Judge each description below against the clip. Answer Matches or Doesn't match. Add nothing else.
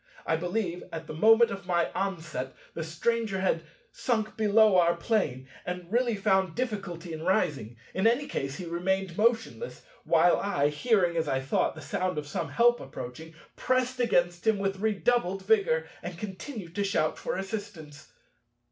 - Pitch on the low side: Doesn't match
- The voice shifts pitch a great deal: Doesn't match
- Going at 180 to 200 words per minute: Doesn't match